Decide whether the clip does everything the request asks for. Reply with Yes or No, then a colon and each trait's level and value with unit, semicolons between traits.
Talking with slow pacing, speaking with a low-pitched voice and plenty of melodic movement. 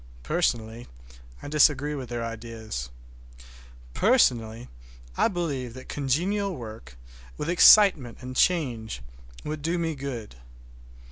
Yes: slow, 110 wpm; low, 130 Hz; wide, 6.0 semitones